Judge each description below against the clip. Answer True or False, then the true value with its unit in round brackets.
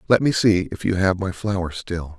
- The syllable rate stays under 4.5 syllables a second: False (5.1 syllables/s)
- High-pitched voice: False (95 Hz)